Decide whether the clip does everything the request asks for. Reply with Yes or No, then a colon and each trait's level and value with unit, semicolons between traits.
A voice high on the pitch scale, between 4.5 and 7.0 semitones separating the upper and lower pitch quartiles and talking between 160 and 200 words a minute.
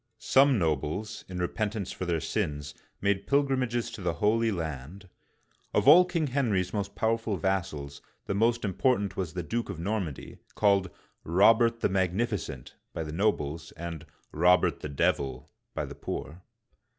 No: very low, 95 Hz; wide, 5.5 semitones; average, 165 wpm